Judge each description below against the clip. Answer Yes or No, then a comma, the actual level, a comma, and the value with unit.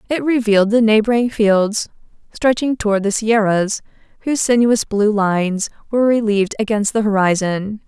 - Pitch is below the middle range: No, high, 215 Hz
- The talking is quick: No, slow, 135 wpm